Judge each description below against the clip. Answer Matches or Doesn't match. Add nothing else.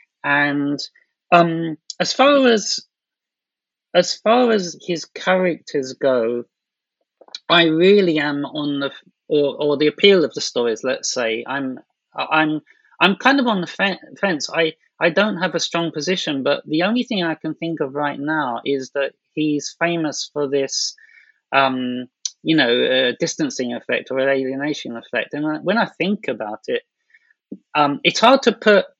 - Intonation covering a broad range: Matches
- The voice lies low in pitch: Doesn't match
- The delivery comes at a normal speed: Matches